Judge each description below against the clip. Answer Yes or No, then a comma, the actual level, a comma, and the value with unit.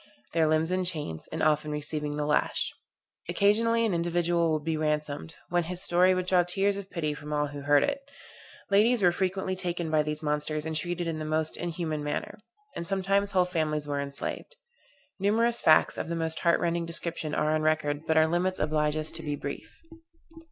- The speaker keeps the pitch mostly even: No, average, 3.0 semitones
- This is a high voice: No, medium, 160 Hz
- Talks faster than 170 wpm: Yes, average, 195 wpm